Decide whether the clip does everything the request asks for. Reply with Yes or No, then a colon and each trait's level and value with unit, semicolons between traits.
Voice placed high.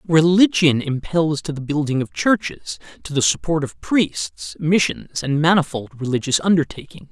No: medium, 150 Hz